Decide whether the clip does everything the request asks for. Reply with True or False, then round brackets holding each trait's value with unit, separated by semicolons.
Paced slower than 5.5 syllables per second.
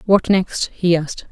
True (4.5 syllables/s)